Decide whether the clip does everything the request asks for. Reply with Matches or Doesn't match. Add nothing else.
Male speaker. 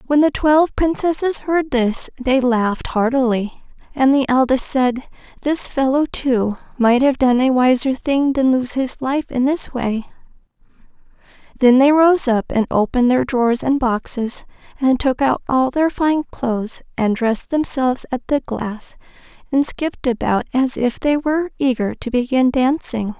Doesn't match